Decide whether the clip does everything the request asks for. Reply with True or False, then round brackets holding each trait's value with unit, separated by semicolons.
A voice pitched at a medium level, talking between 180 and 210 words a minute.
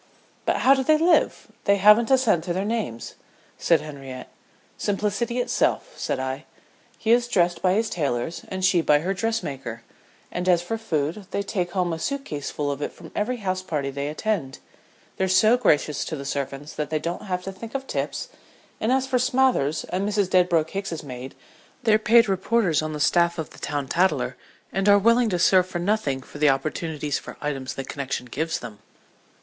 True (180 Hz; 200 wpm)